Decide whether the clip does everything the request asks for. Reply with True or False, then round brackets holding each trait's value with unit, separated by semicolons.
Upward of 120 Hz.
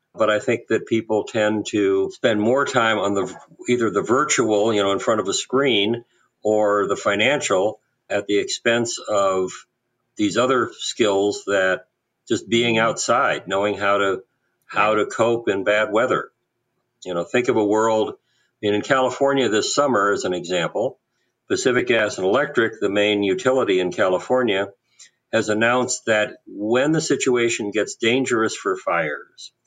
False (110 Hz)